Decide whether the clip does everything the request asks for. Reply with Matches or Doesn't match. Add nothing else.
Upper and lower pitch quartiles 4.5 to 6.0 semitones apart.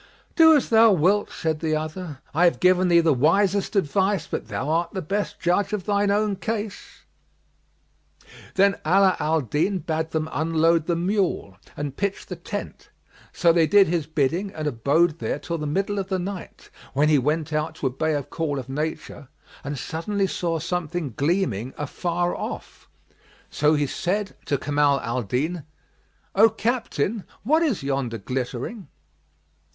Matches